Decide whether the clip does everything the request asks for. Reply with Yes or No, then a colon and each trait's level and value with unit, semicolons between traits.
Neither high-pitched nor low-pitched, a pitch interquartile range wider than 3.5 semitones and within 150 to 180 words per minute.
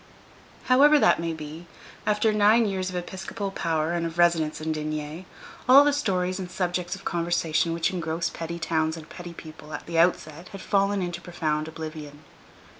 No: medium, 170 Hz; average, 3.0 semitones; average, 175 wpm